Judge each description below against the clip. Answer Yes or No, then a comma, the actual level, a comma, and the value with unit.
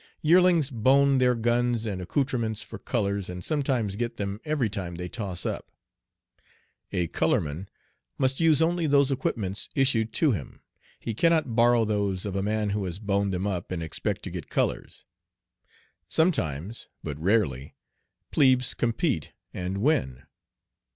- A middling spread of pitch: No, wide, 5.7 semitones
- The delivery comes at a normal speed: Yes, average, 150 wpm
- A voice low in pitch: Yes, low, 110 Hz